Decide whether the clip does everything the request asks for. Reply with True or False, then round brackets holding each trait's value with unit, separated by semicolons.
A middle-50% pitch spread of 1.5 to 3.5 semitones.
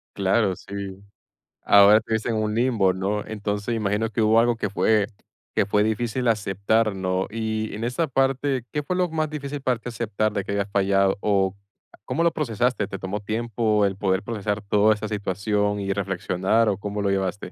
True (2.5 semitones)